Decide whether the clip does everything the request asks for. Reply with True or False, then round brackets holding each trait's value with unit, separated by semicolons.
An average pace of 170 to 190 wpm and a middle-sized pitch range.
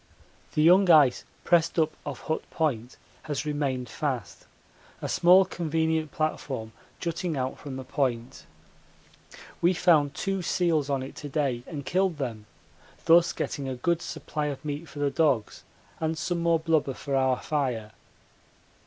False (155 wpm; 3.7 semitones)